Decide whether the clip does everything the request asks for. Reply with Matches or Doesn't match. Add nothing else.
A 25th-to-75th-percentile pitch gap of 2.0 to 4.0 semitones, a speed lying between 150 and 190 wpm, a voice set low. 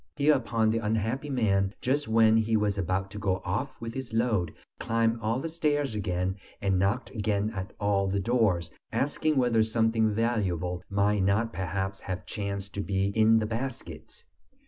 Matches